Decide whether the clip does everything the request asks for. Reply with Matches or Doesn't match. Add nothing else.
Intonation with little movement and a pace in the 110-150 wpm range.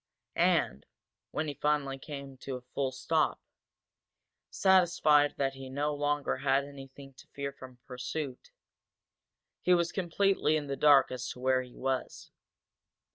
Matches